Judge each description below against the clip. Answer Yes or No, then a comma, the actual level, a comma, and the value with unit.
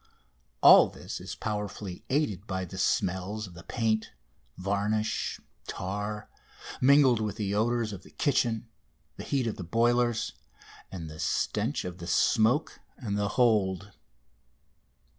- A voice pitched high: No, low, 105 Hz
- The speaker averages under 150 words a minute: Yes, slow, 135 wpm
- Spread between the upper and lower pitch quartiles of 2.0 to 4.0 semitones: Yes, average, 3.6 semitones